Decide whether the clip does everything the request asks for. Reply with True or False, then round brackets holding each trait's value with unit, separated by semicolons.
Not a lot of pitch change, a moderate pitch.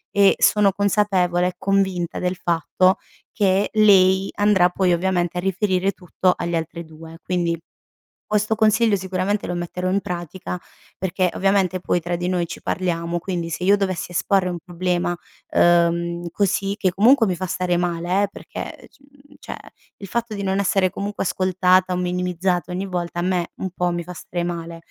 True (2.0 semitones; 180 Hz)